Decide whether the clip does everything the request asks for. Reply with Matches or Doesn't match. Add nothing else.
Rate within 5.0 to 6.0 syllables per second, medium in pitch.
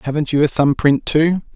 Matches